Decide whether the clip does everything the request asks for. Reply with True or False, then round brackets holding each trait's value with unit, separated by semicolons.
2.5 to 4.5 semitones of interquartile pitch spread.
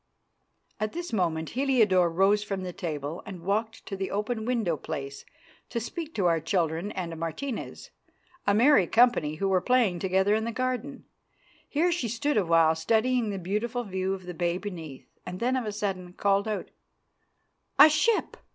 False (5.0 semitones)